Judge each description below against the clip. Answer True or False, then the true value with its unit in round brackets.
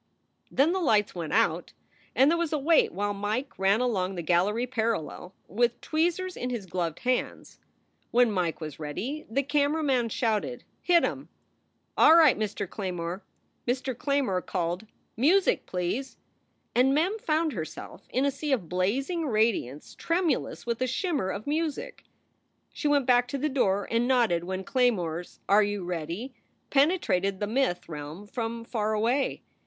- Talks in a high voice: True (235 Hz)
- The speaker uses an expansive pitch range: True (6.8 semitones)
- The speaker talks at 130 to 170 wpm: True (160 wpm)